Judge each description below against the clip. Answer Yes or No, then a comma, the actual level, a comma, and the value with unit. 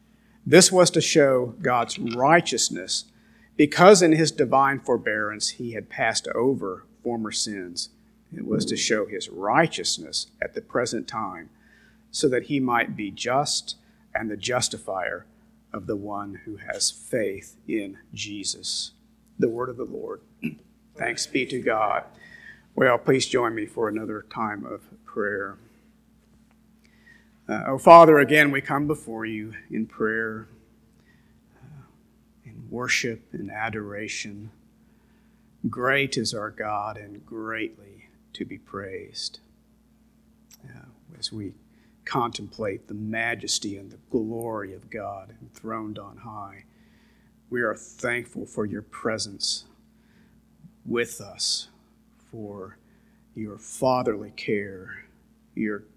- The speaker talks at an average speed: No, slow, 120 wpm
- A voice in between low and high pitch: No, low, 115 Hz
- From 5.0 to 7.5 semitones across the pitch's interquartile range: Yes, wide, 5.6 semitones